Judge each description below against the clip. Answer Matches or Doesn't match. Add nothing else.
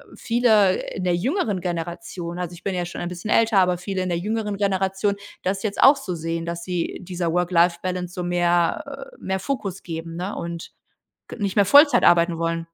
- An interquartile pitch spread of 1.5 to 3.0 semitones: Matches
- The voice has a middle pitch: Matches